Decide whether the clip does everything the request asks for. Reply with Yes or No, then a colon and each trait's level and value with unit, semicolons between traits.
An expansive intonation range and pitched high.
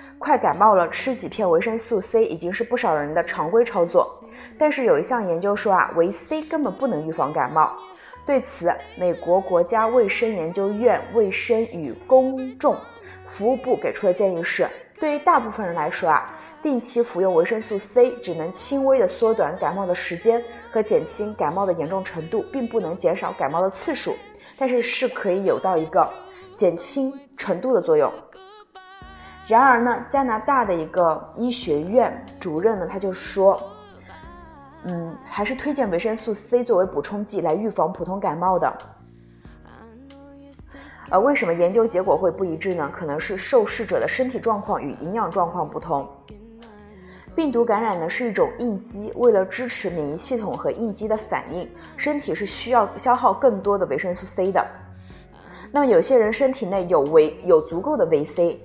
Yes: wide, 6.7 semitones; high, 225 Hz